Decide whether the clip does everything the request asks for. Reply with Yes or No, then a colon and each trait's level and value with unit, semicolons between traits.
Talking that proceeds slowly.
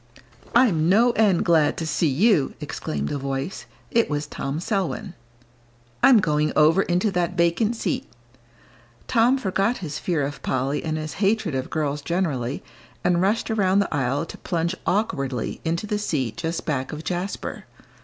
No: average, 160 wpm